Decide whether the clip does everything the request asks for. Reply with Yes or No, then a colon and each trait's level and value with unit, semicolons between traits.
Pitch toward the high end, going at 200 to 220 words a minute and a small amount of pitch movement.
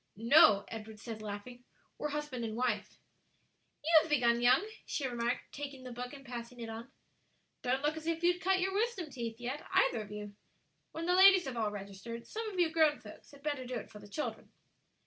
No: very high, 250 Hz; fast, 205 wpm; average, 5.3 semitones